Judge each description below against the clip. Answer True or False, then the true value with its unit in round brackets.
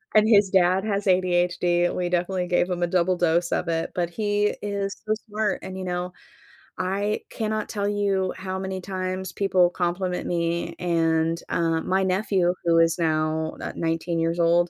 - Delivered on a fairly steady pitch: True (2.2 semitones)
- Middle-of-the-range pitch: True (180 Hz)